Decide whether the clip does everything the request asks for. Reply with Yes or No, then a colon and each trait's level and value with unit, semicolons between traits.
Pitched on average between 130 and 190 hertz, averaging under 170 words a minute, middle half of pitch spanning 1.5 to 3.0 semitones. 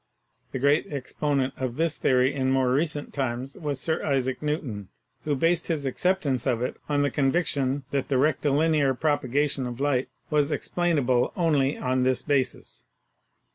Yes: medium, 140 Hz; average, 155 wpm; narrow, 2.5 semitones